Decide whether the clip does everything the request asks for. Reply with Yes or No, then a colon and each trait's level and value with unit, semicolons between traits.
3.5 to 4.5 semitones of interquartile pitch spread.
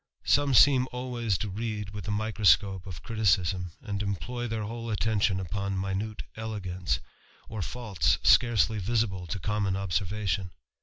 No: average, 2.8 semitones